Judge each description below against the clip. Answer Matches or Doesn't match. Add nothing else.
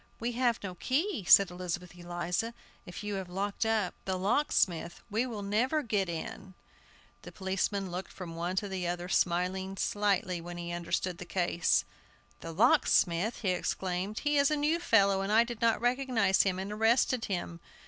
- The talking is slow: Doesn't match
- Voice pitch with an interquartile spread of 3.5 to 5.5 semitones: Matches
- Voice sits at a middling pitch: Doesn't match